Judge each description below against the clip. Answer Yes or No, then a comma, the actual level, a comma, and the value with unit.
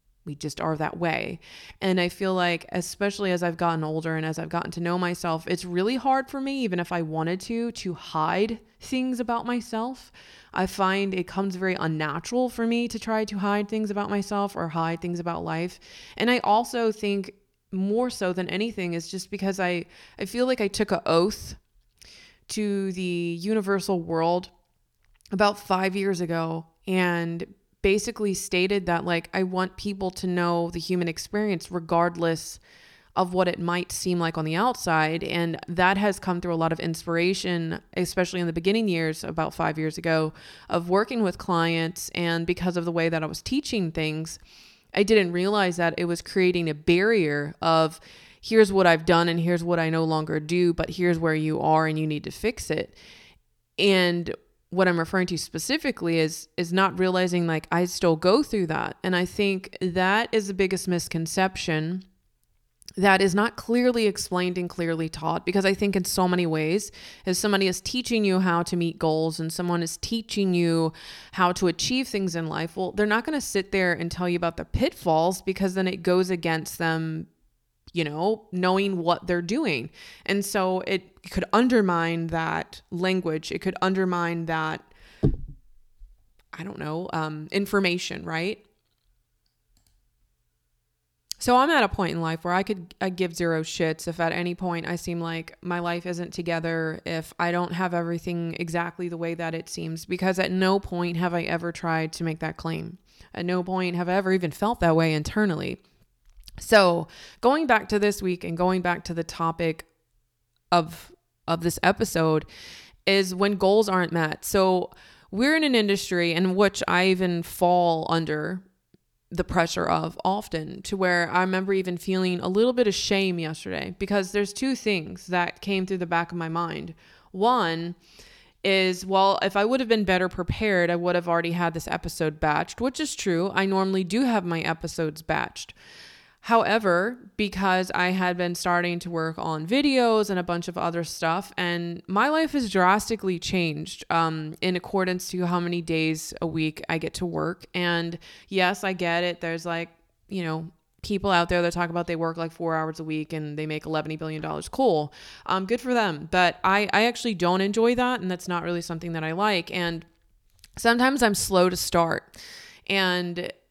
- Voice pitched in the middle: Yes, medium, 180 Hz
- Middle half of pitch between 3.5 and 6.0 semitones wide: No, average, 2.8 semitones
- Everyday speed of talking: Yes, average, 185 wpm